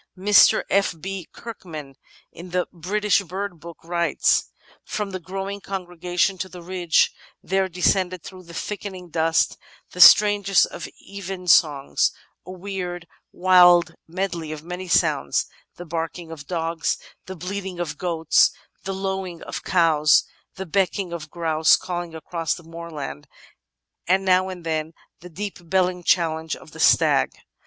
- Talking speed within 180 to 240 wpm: No, average, 145 wpm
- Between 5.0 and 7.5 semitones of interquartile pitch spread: No, narrow, 2.5 semitones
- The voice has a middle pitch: Yes, medium, 180 Hz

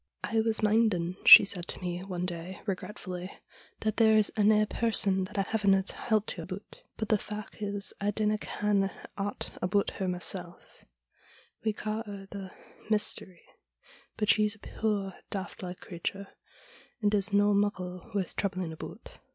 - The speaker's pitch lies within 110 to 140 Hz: No, high, 200 Hz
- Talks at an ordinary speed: Yes, average, 160 wpm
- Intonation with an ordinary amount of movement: No, narrow, 2.3 semitones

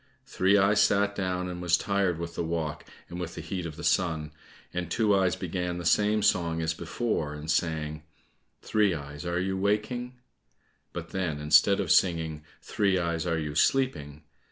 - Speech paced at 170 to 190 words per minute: Yes, average, 180 wpm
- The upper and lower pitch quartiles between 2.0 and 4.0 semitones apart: Yes, average, 3.6 semitones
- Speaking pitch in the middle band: No, very low, 90 Hz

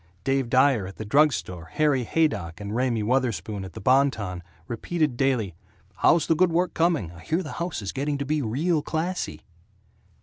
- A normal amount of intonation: No, wide, 6.6 semitones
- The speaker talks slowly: No, average, 190 wpm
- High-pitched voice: No, low, 135 Hz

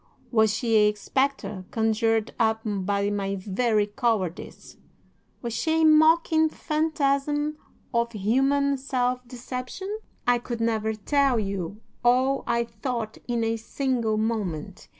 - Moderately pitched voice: No, high, 235 Hz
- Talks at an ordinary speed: No, slow, 125 wpm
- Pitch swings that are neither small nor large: Yes, average, 4.2 semitones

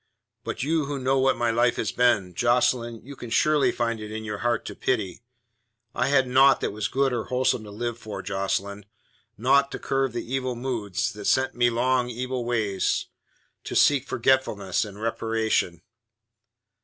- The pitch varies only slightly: No, average, 3.3 semitones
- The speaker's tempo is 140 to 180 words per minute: Yes, average, 175 wpm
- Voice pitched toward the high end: No, low, 120 Hz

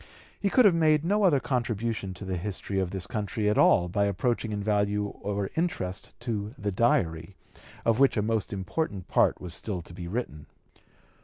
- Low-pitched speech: Yes, low, 105 Hz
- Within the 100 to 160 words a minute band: No, average, 180 wpm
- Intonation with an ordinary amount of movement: Yes, average, 4.0 semitones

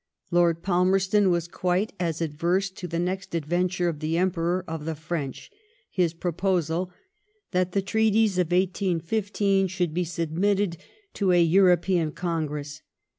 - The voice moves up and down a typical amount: No, narrow, 2.3 semitones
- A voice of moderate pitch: Yes, medium, 175 Hz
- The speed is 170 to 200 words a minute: No, slow, 135 wpm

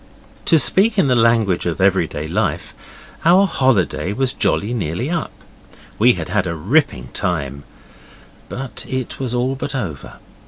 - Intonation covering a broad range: Yes, wide, 7.0 semitones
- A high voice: No, low, 115 Hz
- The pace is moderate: Yes, average, 150 wpm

